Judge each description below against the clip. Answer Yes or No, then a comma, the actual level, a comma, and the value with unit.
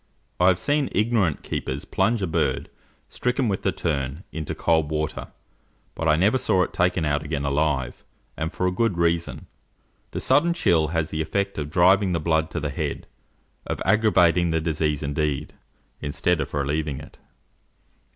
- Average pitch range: Yes, average, 3.7 semitones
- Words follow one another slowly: No, average, 170 wpm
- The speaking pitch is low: Yes, very low, 80 Hz